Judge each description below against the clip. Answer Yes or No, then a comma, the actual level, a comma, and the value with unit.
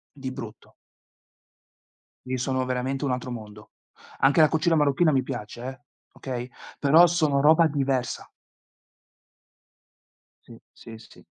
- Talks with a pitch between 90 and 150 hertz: Yes, low, 135 Hz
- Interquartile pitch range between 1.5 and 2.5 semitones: No, average, 2.9 semitones